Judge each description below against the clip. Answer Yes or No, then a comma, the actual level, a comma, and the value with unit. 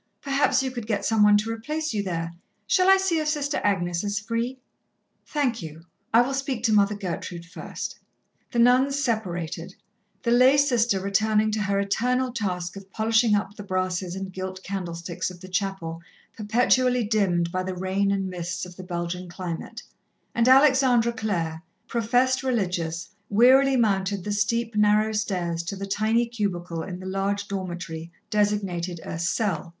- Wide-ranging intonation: No, average, 4.5 semitones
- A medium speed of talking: Yes, average, 165 wpm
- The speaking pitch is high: Yes, high, 205 Hz